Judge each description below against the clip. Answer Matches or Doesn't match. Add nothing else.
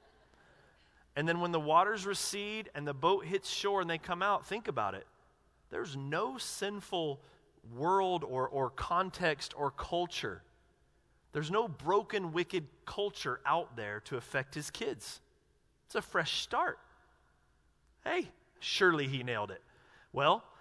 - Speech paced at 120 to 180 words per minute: Matches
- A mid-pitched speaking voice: Matches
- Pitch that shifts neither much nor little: Doesn't match